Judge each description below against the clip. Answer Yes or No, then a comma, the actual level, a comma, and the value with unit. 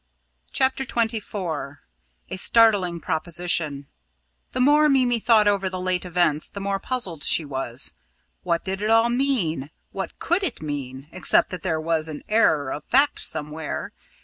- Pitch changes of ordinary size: No, wide, 6.5 semitones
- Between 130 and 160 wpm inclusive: Yes, average, 150 wpm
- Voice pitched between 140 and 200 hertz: Yes, medium, 185 Hz